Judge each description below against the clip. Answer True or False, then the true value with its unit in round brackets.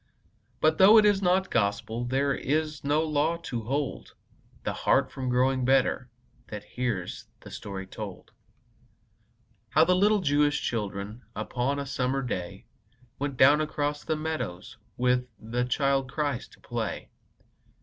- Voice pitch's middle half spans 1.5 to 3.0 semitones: False (3.9 semitones)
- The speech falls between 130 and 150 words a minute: True (140 wpm)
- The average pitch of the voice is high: False (135 Hz)